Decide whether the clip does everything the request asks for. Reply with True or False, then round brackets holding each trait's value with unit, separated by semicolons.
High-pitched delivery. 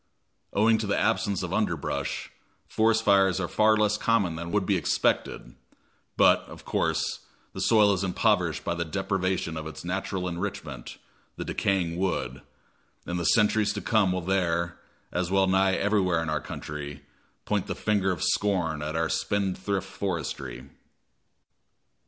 False (95 Hz)